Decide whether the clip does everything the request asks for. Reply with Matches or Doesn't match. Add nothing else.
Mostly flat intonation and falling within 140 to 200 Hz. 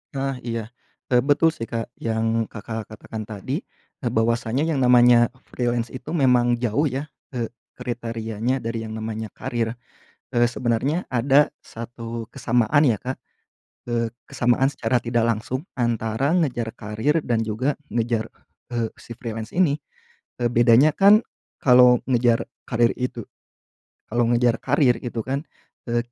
Doesn't match